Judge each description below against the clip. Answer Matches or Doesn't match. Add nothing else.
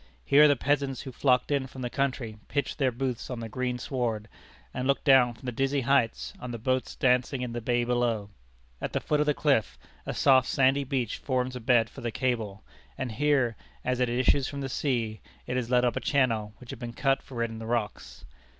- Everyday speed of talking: Doesn't match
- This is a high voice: Doesn't match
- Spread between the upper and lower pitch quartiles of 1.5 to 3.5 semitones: Matches